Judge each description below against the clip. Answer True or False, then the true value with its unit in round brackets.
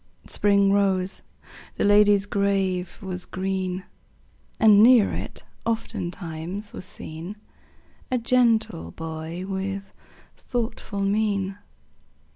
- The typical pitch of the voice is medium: False (195 Hz)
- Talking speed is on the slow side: True (90 wpm)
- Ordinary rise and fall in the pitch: False (2.0 semitones)